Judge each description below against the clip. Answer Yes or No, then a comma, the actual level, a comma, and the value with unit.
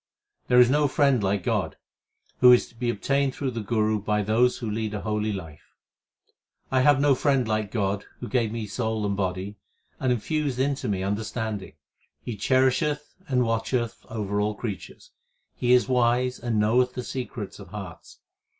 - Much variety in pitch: No, average, 3.4 semitones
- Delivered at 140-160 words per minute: No, average, 175 wpm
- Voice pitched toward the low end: Yes, low, 115 Hz